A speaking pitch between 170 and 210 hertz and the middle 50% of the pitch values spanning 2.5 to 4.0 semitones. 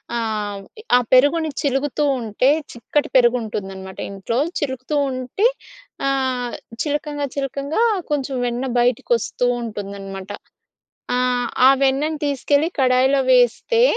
No: very high, 255 Hz; average, 3.6 semitones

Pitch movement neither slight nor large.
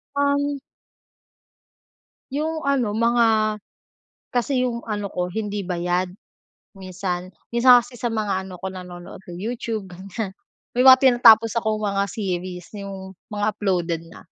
Yes: average, 4.4 semitones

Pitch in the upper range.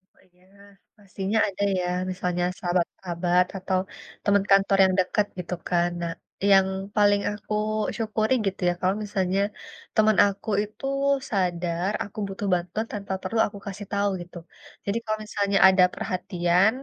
Yes: high, 195 Hz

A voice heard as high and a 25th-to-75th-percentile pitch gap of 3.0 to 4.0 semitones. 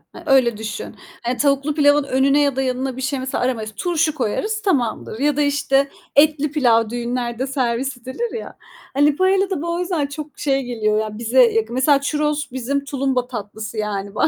Yes: very high, 270 Hz; average, 3.7 semitones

